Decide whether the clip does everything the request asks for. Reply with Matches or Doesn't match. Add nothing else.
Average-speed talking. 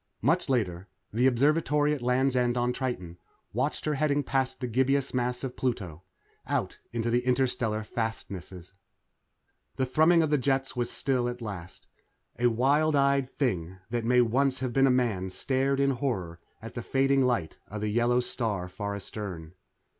Matches